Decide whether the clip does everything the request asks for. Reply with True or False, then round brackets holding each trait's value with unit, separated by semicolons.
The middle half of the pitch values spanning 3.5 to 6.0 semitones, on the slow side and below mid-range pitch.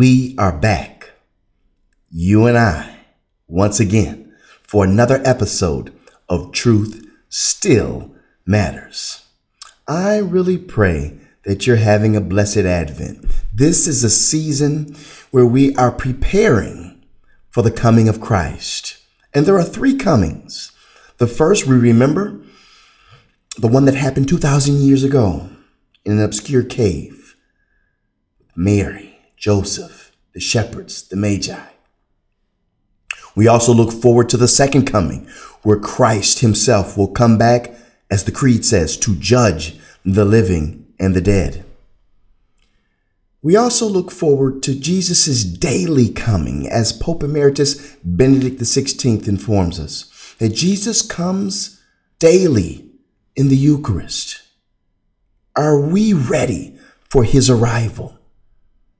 True (5.2 semitones; 120 wpm; 115 Hz)